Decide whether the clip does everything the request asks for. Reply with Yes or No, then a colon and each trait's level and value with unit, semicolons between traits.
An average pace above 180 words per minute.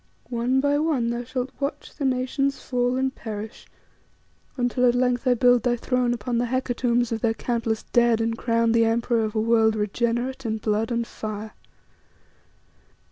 No: average, 170 wpm